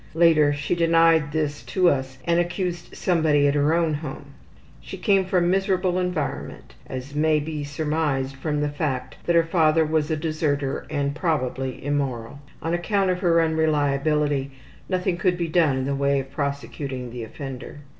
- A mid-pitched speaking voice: Yes, medium, 150 Hz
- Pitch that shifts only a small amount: No, average, 3.0 semitones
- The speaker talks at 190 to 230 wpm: No, average, 165 wpm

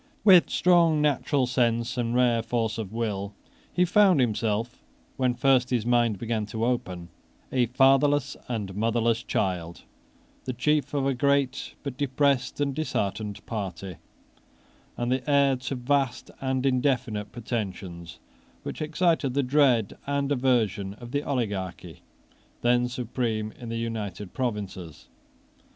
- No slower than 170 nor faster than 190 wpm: No, slow, 135 wpm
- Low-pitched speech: Yes, low, 120 Hz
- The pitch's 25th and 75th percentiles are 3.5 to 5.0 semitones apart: Yes, average, 4.0 semitones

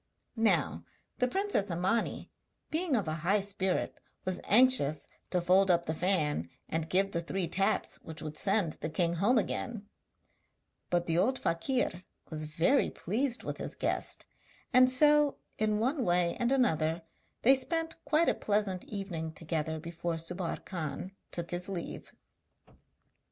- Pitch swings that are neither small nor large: No, wide, 6.1 semitones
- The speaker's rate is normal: Yes, average, 150 wpm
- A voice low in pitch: No, medium, 185 Hz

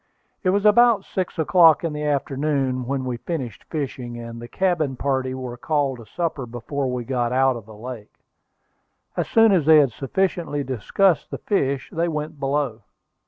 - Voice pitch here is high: No, medium, 140 Hz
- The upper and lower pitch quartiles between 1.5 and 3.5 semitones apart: No, average, 4.5 semitones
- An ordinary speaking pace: Yes, average, 175 wpm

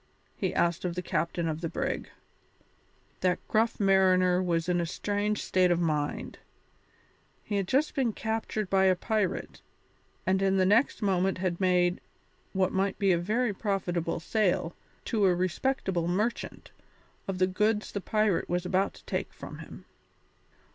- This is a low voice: No, high, 190 Hz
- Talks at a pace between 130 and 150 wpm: No, average, 160 wpm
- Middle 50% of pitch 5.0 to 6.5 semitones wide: No, average, 2.8 semitones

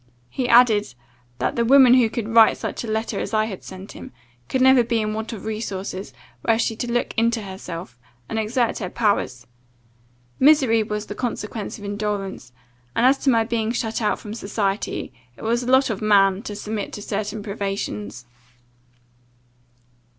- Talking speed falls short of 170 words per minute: No, average, 175 wpm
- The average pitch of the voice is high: Yes, high, 220 Hz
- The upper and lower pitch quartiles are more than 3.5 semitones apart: No, narrow, 2.6 semitones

